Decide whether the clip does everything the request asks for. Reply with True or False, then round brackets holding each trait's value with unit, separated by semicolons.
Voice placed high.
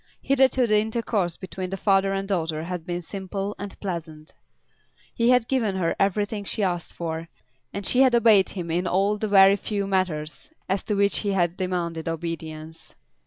True (195 Hz)